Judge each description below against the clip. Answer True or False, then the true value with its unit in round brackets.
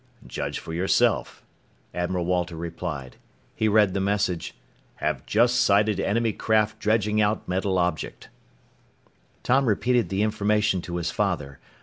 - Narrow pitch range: False (3.3 semitones)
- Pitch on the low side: True (100 Hz)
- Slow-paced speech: True (130 wpm)